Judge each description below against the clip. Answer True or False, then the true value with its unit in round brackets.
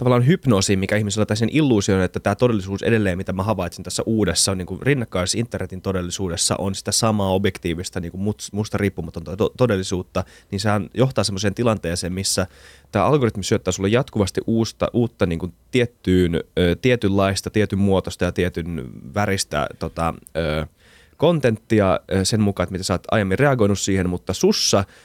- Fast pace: True (165 wpm)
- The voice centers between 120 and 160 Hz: False (100 Hz)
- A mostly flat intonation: False (3.2 semitones)